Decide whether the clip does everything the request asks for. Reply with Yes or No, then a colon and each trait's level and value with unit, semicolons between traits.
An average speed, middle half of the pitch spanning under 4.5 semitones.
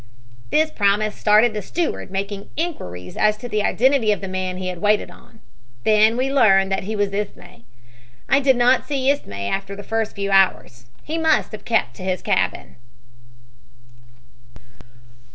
Yes: average, 165 wpm; average, 4.1 semitones